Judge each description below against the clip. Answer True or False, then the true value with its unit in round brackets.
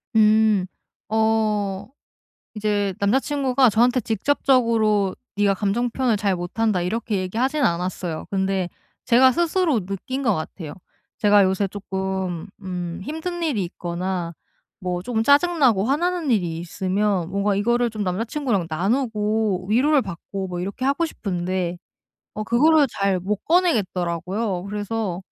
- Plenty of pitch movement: False (4.5 semitones)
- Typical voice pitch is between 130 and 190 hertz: False (210 Hz)